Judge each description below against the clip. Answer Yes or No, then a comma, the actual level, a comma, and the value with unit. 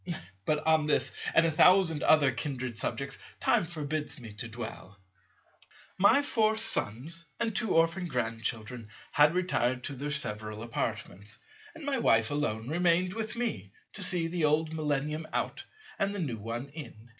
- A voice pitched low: No, medium, 150 Hz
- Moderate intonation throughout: No, wide, 6.6 semitones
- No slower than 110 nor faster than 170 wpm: Yes, average, 155 wpm